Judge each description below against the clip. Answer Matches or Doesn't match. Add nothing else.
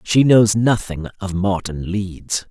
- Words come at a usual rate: Matches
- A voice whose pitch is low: Matches